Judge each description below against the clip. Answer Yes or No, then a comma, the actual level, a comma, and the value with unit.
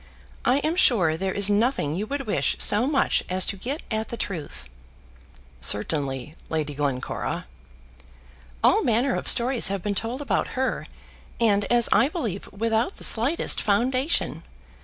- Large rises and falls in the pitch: Yes, wide, 5.7 semitones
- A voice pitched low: No, high, 220 Hz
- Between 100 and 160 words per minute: Yes, average, 150 wpm